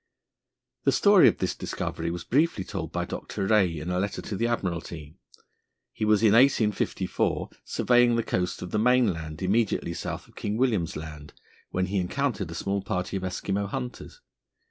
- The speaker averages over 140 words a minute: Yes, average, 170 wpm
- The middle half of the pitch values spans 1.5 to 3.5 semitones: No, average, 4.8 semitones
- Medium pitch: No, low, 100 Hz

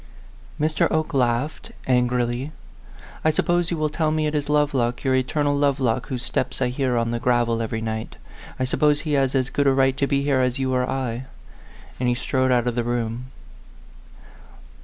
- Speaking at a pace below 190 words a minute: No, average, 195 wpm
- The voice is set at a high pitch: No, low, 130 Hz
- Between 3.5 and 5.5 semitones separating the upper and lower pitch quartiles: No, average, 3.0 semitones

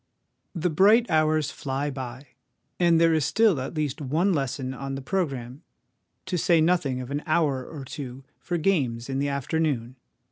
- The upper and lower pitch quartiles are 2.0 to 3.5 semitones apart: No, average, 3.9 semitones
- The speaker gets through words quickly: No, average, 170 wpm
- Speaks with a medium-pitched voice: Yes, medium, 145 Hz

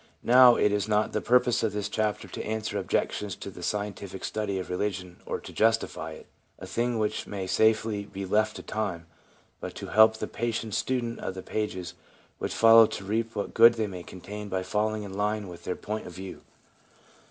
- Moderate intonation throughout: No, narrow, 2.3 semitones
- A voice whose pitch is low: Yes, low, 105 Hz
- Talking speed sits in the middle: No, fast, 210 wpm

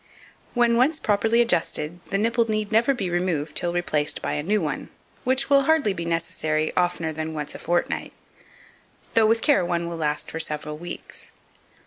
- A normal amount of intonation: No, wide, 6.1 semitones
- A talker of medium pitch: Yes, medium, 175 Hz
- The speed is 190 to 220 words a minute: No, average, 175 wpm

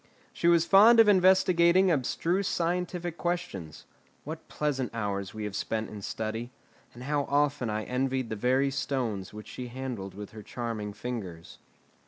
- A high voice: No, low, 130 Hz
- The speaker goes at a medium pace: Yes, average, 155 wpm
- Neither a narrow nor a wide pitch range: No, wide, 7.9 semitones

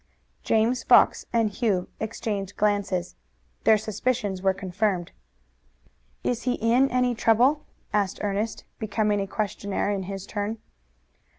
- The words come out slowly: Yes, slow, 120 wpm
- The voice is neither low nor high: No, high, 210 Hz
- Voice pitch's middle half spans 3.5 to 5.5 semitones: No, narrow, 2.5 semitones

